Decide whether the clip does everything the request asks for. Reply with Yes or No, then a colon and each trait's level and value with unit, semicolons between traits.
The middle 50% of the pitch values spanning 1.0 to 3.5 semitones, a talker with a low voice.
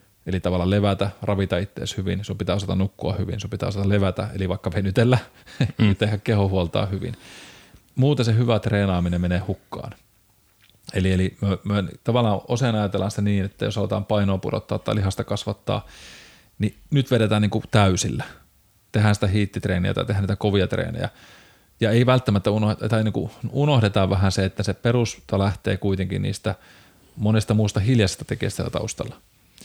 Yes: narrow, 2.4 semitones; low, 105 Hz